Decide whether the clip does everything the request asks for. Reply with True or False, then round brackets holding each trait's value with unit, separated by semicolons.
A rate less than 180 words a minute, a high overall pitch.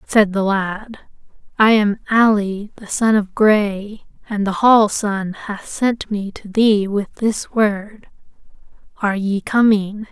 True (150 wpm; 205 Hz)